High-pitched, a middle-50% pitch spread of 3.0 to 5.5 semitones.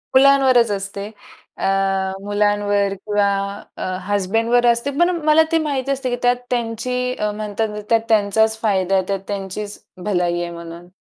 Yes: high, 210 Hz; average, 3.5 semitones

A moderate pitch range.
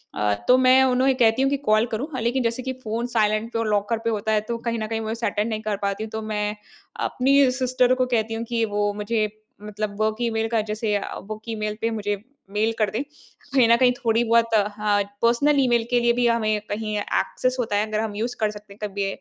No: narrow, 2.1 semitones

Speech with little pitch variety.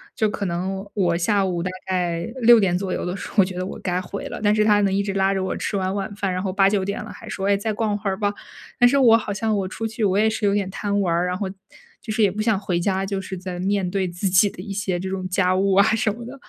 Yes: narrow, 1.9 semitones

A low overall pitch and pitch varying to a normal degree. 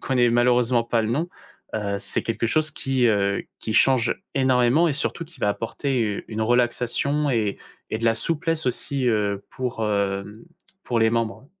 Yes: low, 120 Hz; average, 3.3 semitones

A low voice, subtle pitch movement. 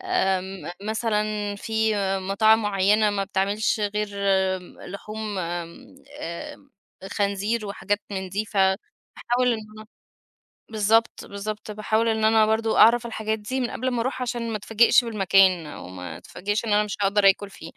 No: high, 210 Hz; narrow, 2.1 semitones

